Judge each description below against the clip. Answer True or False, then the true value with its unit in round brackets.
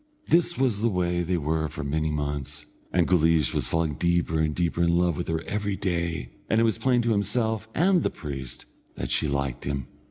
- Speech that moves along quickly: True (210 wpm)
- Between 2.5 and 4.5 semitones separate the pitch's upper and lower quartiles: False (5.4 semitones)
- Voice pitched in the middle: False (85 Hz)